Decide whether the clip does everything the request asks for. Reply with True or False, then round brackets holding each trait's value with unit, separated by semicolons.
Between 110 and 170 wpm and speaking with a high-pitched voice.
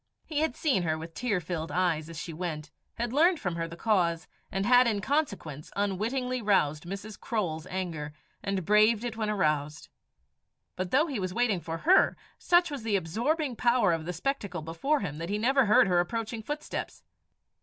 False (185 wpm; 200 Hz)